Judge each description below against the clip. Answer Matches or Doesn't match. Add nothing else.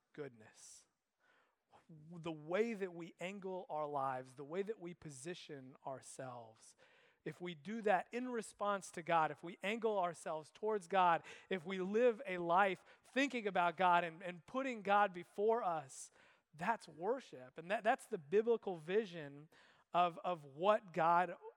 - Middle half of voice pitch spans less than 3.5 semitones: Doesn't match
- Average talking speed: Matches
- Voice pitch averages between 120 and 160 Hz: Doesn't match